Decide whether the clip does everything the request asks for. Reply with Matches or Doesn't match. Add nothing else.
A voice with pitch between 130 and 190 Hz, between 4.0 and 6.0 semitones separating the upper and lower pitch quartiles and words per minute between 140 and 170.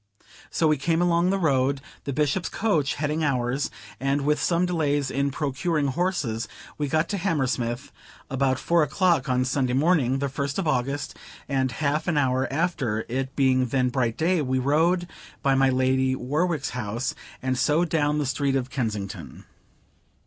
Doesn't match